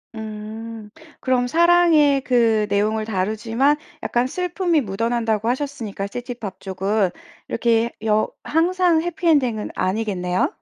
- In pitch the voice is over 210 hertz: Yes, high, 230 Hz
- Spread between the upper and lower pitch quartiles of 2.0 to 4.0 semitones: No, average, 5.3 semitones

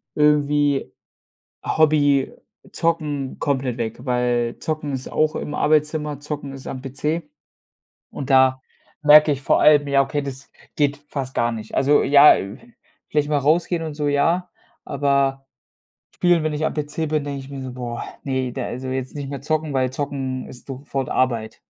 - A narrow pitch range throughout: Yes, narrow, 2.3 semitones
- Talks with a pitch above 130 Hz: Yes, medium, 140 Hz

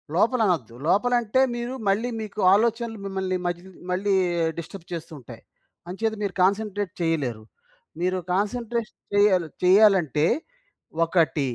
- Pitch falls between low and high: No, high, 195 Hz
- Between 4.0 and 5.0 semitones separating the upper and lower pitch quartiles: Yes, average, 4.4 semitones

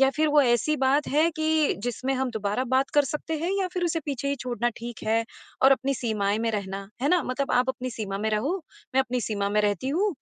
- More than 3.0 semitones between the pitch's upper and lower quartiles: Yes, average, 5.0 semitones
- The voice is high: Yes, very high, 260 Hz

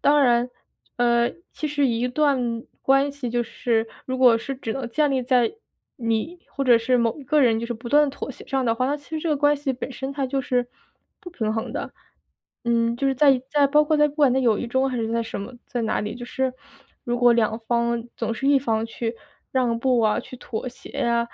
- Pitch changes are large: No, average, 2.9 semitones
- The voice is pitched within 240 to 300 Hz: Yes, very high, 250 Hz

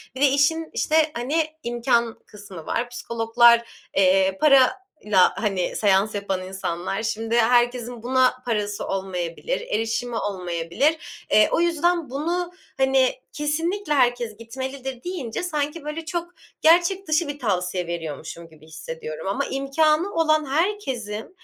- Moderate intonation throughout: No, wide, 7.2 semitones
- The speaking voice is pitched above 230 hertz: Yes, high, 245 Hz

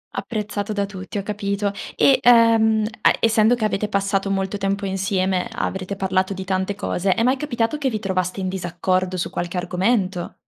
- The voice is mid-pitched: No, high, 195 Hz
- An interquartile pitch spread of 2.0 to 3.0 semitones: Yes, narrow, 2.5 semitones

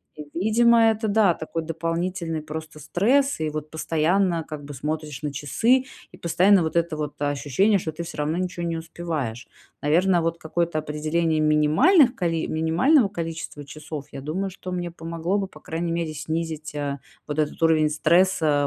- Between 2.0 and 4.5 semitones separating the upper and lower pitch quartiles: Yes, average, 2.9 semitones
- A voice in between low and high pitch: Yes, medium, 165 Hz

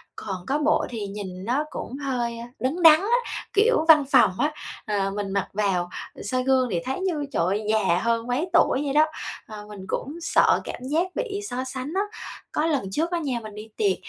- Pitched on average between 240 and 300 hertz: Yes, very high, 255 Hz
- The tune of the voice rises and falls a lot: Yes, wide, 6.7 semitones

